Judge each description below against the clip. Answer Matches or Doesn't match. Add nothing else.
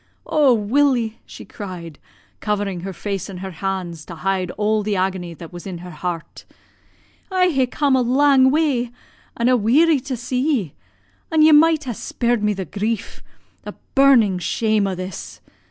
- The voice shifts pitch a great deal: Matches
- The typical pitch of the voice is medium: Doesn't match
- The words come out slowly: Doesn't match